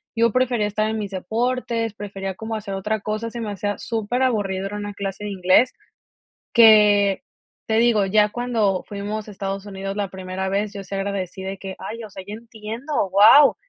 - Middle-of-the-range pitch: No, high, 210 Hz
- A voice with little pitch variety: Yes, narrow, 2.3 semitones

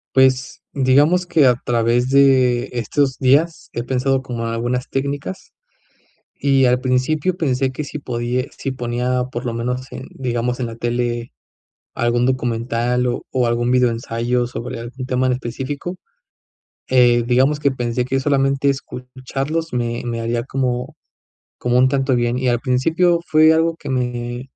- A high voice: No, low, 125 Hz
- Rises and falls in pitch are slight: Yes, narrow, 1.9 semitones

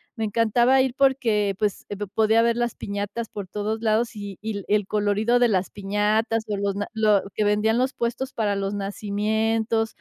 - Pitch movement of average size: No, narrow, 2.0 semitones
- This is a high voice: Yes, high, 215 Hz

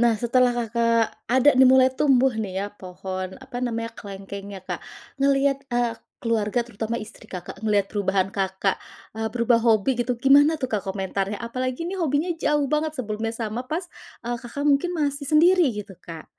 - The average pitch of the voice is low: No, high, 235 Hz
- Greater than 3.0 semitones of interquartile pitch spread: Yes, average, 4.7 semitones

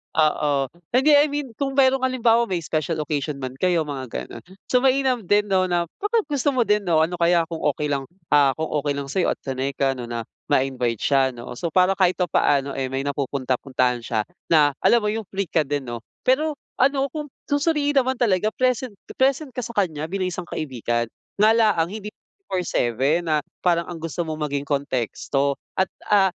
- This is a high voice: No, medium, 170 Hz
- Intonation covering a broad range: Yes, wide, 8.8 semitones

